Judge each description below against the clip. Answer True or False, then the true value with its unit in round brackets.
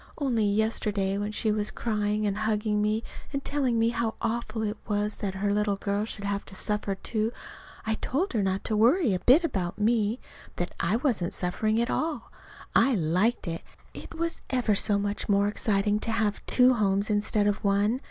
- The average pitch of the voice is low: False (210 Hz)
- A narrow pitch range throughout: True (2.2 semitones)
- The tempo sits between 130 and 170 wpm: False (190 wpm)